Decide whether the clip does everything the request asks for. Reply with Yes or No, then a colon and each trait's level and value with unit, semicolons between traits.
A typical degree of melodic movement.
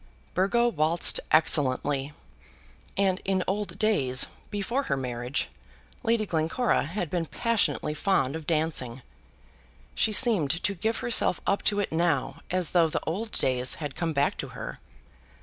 No: wide, 5.8 semitones